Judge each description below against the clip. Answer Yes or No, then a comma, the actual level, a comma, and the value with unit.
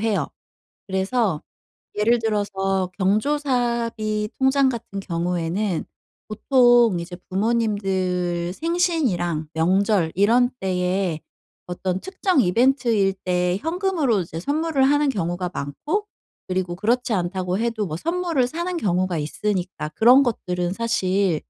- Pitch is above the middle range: Yes, high, 205 Hz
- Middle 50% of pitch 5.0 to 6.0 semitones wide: Yes, wide, 5.5 semitones